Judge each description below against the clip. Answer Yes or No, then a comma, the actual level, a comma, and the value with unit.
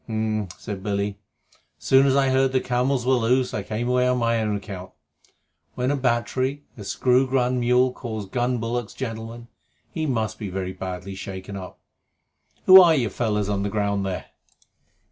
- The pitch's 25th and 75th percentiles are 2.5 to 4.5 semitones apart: Yes, average, 3.9 semitones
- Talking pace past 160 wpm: Yes, average, 180 wpm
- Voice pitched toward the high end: No, low, 115 Hz